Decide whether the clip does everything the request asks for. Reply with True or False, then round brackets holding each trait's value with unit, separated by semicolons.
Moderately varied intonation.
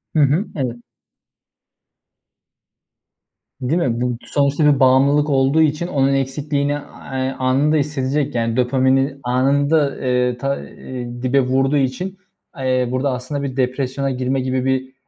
False (1.9 semitones)